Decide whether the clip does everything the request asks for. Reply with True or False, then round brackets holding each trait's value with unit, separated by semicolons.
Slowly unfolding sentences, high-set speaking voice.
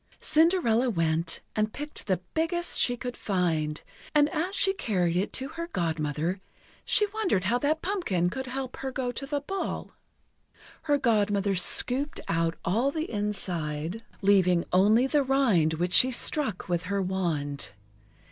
False (150 wpm; 215 Hz)